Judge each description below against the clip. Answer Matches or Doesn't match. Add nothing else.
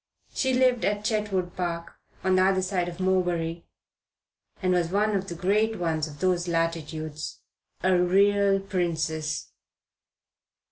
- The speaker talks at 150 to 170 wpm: Doesn't match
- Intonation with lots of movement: Doesn't match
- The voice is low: Doesn't match